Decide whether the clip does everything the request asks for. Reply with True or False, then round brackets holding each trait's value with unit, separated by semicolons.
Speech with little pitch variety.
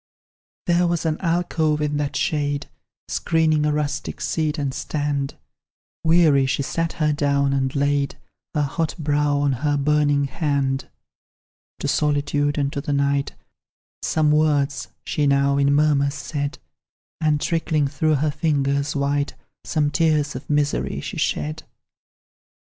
True (1.5 semitones)